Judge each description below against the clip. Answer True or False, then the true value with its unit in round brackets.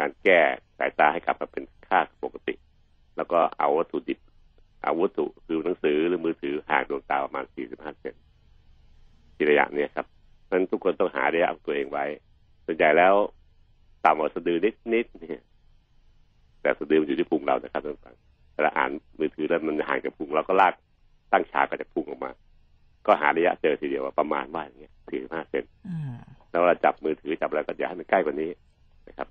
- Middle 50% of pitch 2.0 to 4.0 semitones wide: True (3.5 semitones)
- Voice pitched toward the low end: False (375 Hz)